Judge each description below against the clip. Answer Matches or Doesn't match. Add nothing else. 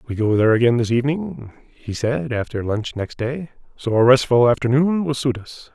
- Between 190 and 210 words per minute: Matches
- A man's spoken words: Matches